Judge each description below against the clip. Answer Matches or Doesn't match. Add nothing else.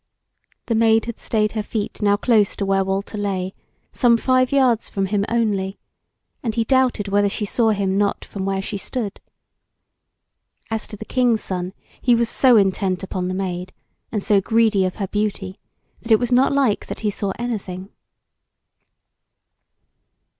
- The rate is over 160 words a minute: Matches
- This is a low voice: Doesn't match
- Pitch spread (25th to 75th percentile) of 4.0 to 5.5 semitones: Doesn't match